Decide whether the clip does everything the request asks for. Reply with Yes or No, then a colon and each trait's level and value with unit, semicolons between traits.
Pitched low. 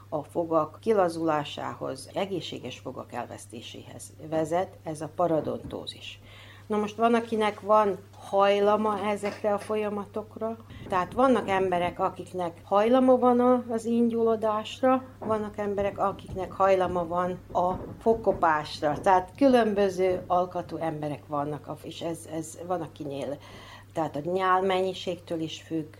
No: medium, 180 Hz